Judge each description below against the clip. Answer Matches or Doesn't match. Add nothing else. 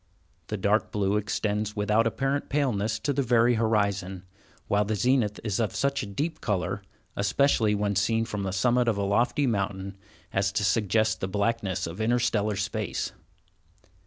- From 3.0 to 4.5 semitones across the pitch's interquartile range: Doesn't match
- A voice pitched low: Matches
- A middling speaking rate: Matches